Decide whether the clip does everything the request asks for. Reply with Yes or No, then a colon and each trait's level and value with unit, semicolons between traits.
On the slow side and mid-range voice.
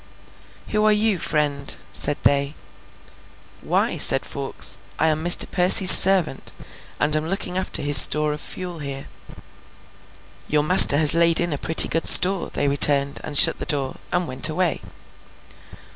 No: average, 155 wpm; medium, 155 Hz